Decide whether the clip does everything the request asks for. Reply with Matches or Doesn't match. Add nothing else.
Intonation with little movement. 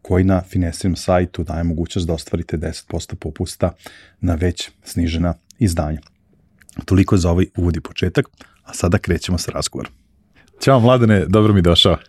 Matches